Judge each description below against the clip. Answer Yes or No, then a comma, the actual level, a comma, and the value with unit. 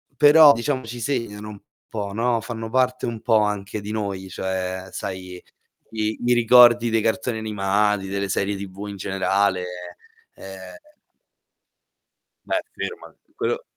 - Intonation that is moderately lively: Yes, average, 3.2 semitones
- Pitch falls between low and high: No, low, 105 Hz